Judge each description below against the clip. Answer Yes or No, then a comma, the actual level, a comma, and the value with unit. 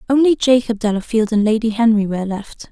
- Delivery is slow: No, average, 175 wpm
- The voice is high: Yes, high, 225 Hz